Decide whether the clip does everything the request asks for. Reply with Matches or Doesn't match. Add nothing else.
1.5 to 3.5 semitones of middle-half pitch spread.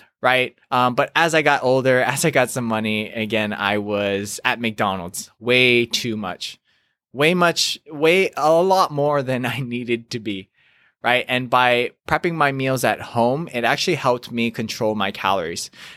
Doesn't match